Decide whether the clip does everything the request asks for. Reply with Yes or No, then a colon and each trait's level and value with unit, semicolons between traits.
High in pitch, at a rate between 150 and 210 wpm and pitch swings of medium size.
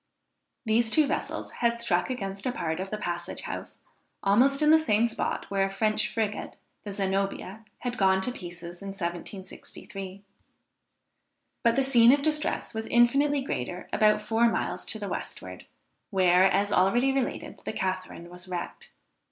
Yes: high, 205 Hz; average, 160 wpm; average, 4.1 semitones